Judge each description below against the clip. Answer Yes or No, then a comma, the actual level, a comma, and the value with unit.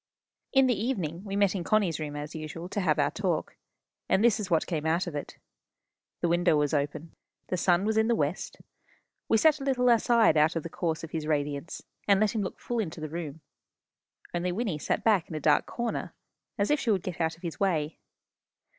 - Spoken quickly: Yes, fast, 220 wpm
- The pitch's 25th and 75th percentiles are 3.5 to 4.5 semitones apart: No, average, 5.2 semitones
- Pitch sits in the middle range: Yes, medium, 175 Hz